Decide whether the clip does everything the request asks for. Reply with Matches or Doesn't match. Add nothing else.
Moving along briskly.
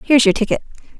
Doesn't match